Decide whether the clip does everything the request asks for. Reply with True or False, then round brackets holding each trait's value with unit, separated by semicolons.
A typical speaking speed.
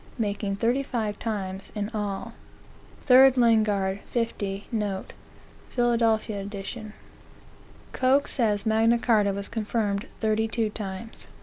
False (110 wpm)